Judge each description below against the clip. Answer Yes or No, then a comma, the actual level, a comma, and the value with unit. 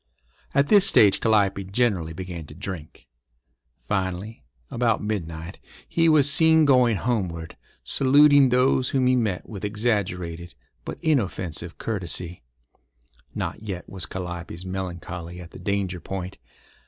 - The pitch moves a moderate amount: No, wide, 5.7 semitones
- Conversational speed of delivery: No, slow, 125 wpm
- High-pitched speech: No, very low, 95 Hz